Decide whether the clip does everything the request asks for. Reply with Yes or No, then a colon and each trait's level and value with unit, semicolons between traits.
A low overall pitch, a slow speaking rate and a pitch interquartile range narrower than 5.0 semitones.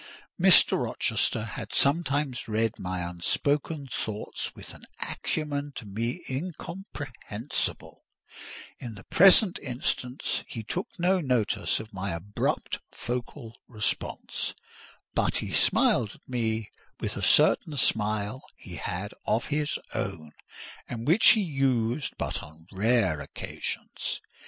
No: low, 120 Hz; slow, 120 wpm; wide, 5.5 semitones